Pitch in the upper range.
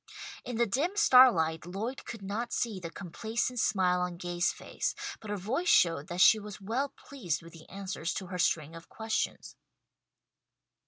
Yes: high, 195 Hz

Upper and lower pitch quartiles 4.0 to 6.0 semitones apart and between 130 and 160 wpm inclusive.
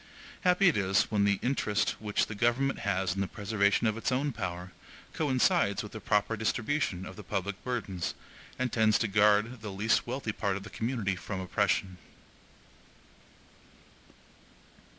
No: average, 3.4 semitones; average, 155 wpm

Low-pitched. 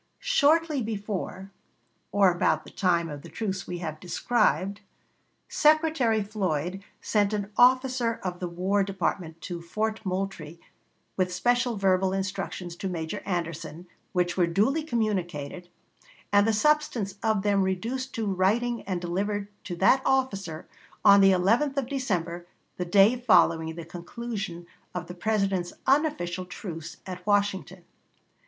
No: high, 195 Hz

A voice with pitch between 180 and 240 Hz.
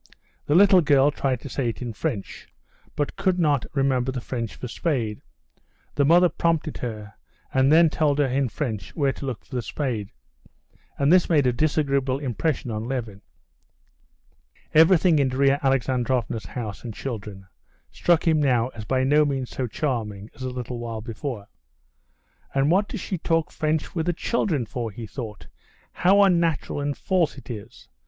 No: low, 135 Hz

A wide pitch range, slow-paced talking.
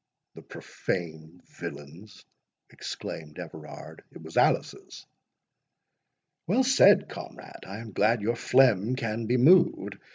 Yes: wide, 6.2 semitones; slow, 105 wpm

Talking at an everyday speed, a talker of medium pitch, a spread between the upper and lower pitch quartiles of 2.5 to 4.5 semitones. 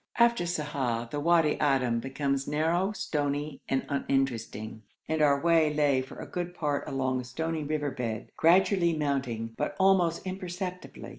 Yes: average, 150 wpm; medium, 150 Hz; average, 4.1 semitones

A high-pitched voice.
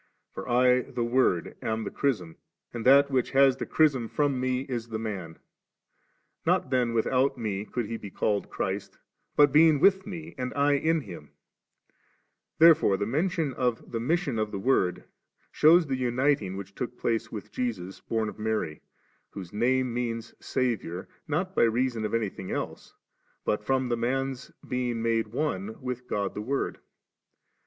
No: low, 120 Hz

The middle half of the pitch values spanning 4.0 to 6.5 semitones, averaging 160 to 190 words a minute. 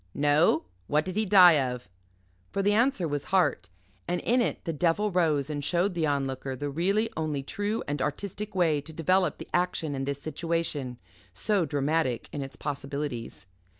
Yes: average, 4.6 semitones; average, 175 wpm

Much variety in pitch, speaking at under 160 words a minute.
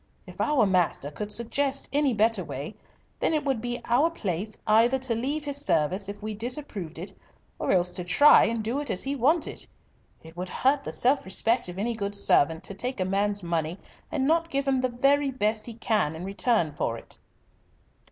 No: wide, 6.2 semitones; average, 200 wpm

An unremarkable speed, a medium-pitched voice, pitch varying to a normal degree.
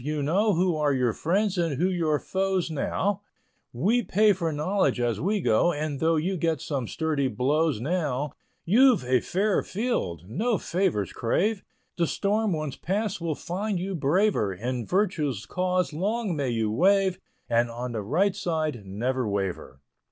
No: average, 165 wpm; medium, 160 Hz; wide, 6.9 semitones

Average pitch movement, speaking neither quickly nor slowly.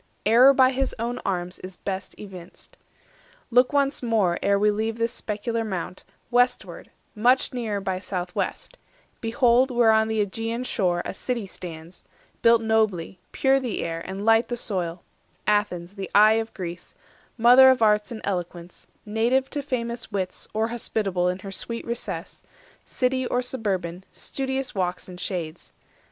Yes: average, 4.5 semitones; average, 160 wpm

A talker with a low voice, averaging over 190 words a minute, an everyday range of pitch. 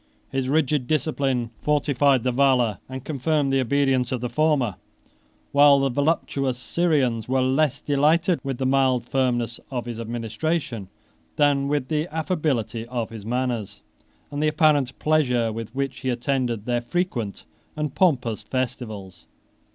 No: low, 130 Hz; average, 145 wpm; average, 3.4 semitones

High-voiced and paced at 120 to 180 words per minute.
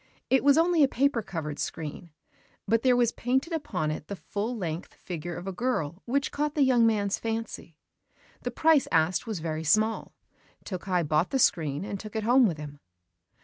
No: high, 210 Hz; average, 190 wpm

